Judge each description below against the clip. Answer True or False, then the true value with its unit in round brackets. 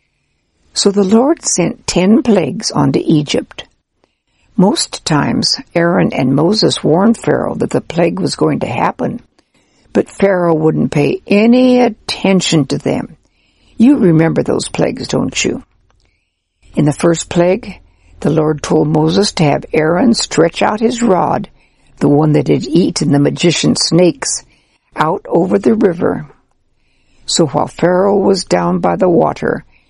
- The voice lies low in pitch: False (170 Hz)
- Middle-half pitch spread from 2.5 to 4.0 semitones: False (4.8 semitones)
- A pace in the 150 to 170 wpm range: False (140 wpm)